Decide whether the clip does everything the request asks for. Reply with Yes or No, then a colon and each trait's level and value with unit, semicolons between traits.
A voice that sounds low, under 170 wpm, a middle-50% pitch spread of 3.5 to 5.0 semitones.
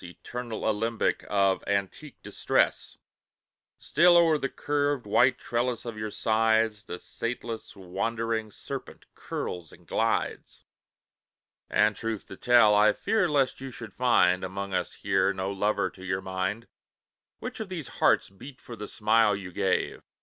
Yes: low, 110 Hz; average, 145 wpm; average, 3.9 semitones